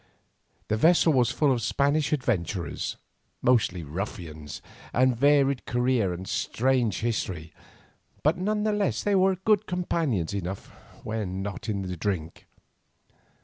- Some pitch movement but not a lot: No, wide, 7.8 semitones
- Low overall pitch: Yes, low, 120 Hz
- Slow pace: Yes, slow, 115 wpm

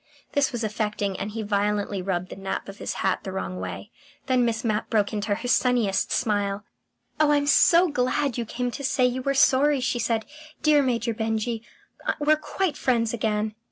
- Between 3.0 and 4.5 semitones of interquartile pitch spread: Yes, average, 3.8 semitones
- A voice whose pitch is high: Yes, high, 230 Hz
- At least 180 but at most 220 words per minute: Yes, average, 190 wpm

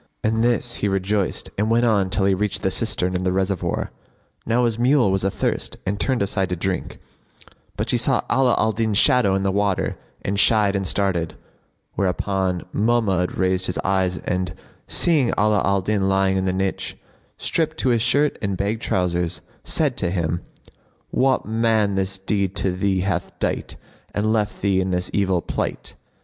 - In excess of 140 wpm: Yes, average, 180 wpm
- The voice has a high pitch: No, low, 100 Hz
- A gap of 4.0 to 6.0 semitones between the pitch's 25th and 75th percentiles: No, average, 2.8 semitones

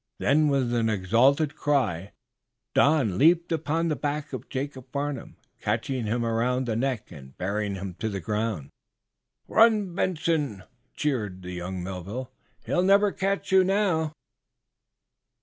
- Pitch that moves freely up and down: Yes, wide, 7.0 semitones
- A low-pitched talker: Yes, low, 130 Hz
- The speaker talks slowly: Yes, slow, 130 wpm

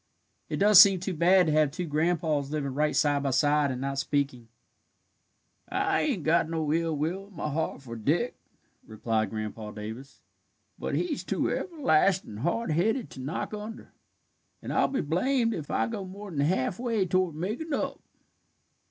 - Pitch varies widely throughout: Yes, wide, 5.8 semitones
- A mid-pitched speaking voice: Yes, medium, 160 Hz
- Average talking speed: Yes, average, 170 wpm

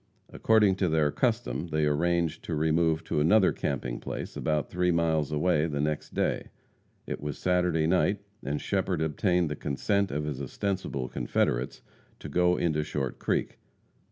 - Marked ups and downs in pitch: No, average, 3.3 semitones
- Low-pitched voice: Yes, very low, 80 Hz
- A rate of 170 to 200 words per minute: No, average, 155 wpm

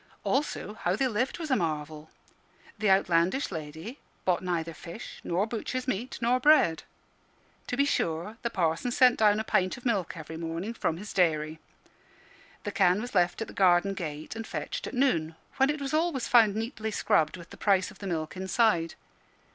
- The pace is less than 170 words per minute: No, average, 185 wpm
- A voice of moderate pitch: No, high, 195 Hz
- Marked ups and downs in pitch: Yes, wide, 6.2 semitones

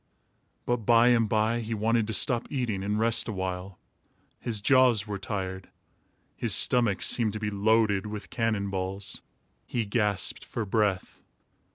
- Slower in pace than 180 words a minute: Yes, average, 155 wpm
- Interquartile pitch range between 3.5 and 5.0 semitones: No, narrow, 2.6 semitones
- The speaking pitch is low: Yes, low, 105 Hz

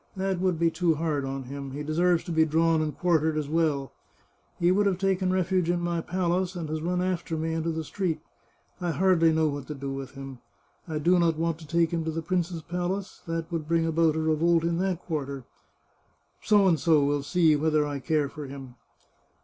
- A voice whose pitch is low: No, medium, 165 Hz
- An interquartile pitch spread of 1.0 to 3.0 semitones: Yes, narrow, 2.5 semitones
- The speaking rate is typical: No, fast, 210 wpm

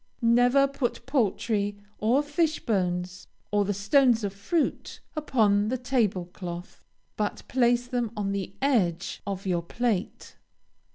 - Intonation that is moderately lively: Yes, average, 4.3 semitones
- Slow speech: Yes, slow, 130 wpm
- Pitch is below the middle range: No, high, 215 Hz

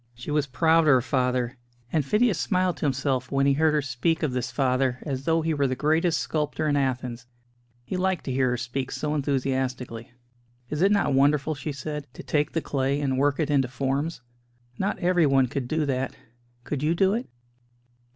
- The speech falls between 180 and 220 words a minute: Yes, average, 200 wpm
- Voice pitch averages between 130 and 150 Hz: Yes, medium, 140 Hz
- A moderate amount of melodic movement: Yes, average, 3.3 semitones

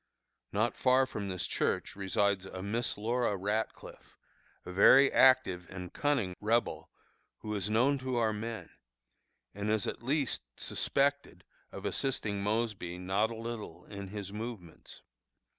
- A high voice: No, low, 105 Hz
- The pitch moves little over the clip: No, average, 3.2 semitones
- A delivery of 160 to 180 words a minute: No, average, 140 wpm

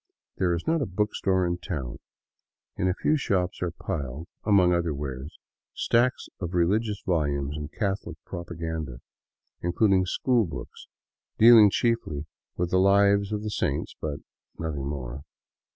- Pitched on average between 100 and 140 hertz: No, very low, 90 Hz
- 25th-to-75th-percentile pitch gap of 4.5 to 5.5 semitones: Yes, average, 5.0 semitones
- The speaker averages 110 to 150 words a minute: Yes, average, 140 wpm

